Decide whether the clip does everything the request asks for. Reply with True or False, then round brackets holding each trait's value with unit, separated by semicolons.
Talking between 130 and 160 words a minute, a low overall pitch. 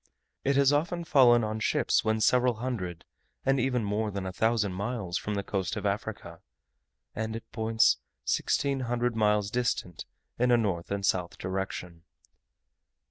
True (155 wpm; 110 Hz)